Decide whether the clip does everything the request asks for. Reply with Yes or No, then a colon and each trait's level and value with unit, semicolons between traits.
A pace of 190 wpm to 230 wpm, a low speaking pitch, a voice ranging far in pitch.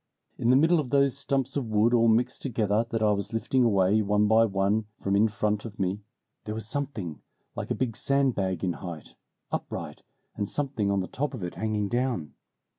No: average, 200 wpm; low, 110 Hz; average, 3.9 semitones